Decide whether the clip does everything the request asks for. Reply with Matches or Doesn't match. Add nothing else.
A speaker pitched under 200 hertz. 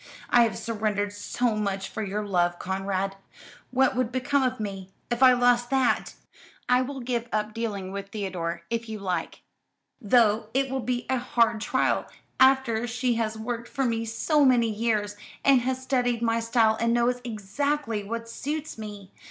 Doesn't match